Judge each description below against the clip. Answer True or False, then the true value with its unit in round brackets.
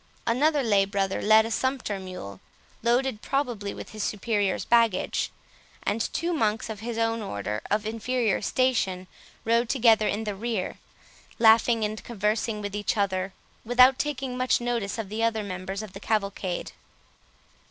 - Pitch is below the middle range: False (220 Hz)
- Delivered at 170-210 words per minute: False (150 wpm)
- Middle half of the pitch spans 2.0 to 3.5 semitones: True (3.0 semitones)